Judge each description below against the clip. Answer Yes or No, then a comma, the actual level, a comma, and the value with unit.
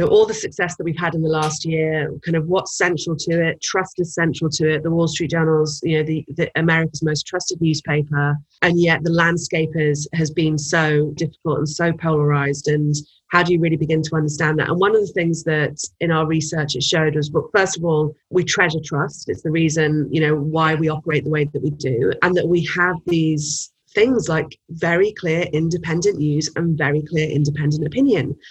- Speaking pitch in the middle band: Yes, medium, 160 Hz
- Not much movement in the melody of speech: Yes, narrow, 1.9 semitones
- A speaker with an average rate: No, fast, 220 wpm